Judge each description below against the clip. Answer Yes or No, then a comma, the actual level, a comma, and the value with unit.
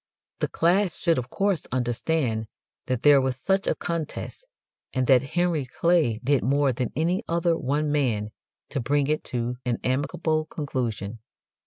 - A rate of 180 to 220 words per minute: No, average, 155 wpm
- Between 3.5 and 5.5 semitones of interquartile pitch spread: Yes, average, 4.7 semitones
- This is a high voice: No, medium, 140 Hz